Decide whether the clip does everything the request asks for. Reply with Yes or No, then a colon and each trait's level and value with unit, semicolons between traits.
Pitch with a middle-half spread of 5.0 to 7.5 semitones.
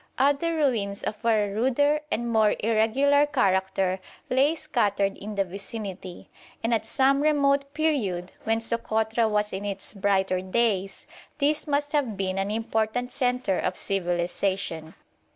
Yes: wide, 5.5 semitones